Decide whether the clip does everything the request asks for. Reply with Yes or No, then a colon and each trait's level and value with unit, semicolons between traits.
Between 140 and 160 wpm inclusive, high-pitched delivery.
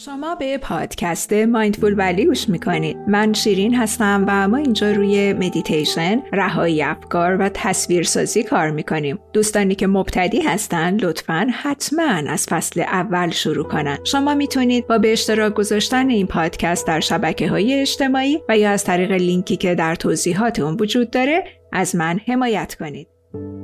Yes: average, 150 wpm; high, 205 Hz